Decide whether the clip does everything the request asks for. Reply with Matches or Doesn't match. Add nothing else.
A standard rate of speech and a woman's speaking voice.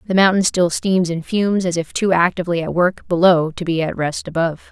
Doesn't match